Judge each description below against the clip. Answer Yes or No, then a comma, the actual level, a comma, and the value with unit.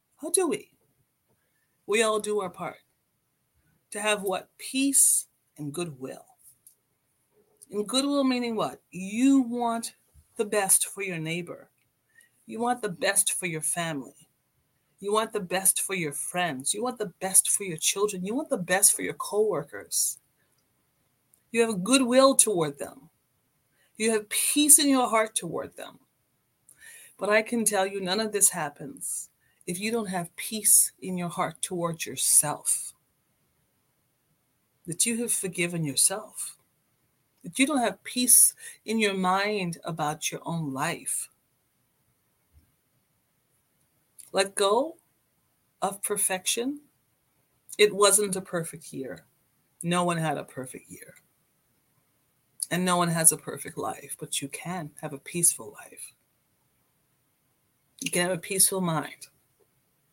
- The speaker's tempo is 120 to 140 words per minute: Yes, slow, 135 wpm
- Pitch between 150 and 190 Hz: Yes, medium, 185 Hz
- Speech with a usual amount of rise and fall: No, wide, 6.2 semitones